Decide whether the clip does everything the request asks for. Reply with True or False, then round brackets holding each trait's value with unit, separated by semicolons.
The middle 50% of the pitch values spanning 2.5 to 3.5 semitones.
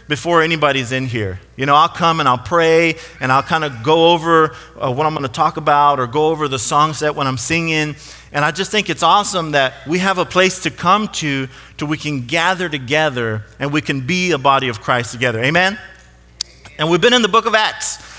False (3.9 semitones)